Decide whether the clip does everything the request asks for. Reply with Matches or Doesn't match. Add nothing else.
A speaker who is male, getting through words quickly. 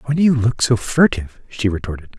Matches